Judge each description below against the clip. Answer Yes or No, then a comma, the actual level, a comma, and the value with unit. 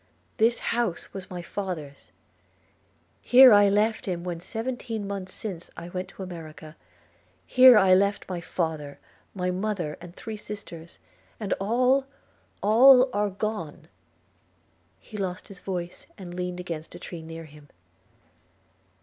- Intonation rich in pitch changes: No, average, 3.8 semitones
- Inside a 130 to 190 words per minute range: Yes, average, 145 wpm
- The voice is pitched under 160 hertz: No, medium, 185 Hz